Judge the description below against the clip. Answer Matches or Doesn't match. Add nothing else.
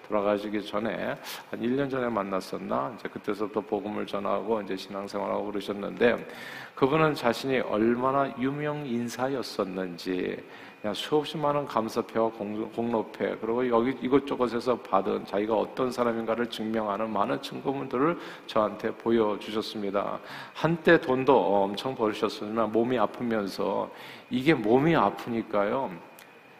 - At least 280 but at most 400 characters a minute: Matches